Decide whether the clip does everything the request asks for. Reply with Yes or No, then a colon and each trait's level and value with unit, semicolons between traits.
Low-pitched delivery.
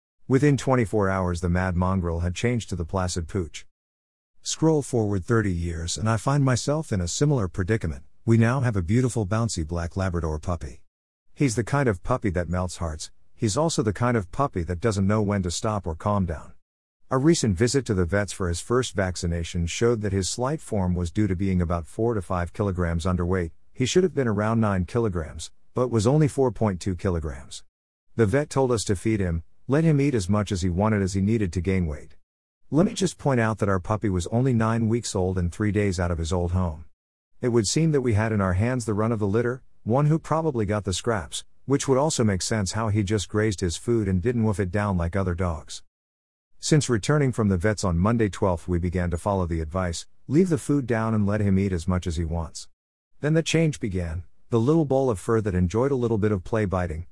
Yes: low, 100 Hz